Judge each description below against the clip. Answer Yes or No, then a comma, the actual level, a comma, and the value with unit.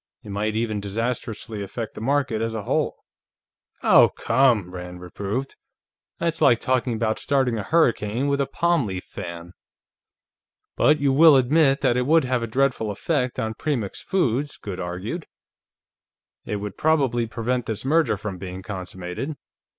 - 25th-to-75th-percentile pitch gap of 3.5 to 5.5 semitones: Yes, average, 5.1 semitones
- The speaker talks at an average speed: Yes, average, 155 wpm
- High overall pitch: No, low, 115 Hz